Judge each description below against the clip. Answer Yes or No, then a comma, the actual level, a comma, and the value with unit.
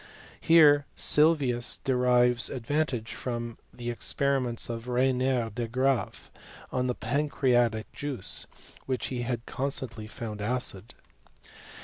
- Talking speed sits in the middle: No, slow, 110 wpm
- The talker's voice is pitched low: Yes, low, 125 Hz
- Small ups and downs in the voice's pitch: Yes, narrow, 2.3 semitones